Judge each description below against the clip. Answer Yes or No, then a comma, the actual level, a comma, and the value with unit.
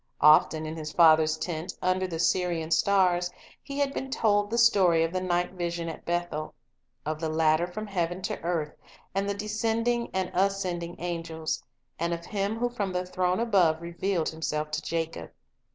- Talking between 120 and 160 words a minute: No, average, 175 wpm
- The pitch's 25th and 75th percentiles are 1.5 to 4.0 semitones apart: Yes, average, 3.4 semitones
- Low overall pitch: No, medium, 175 Hz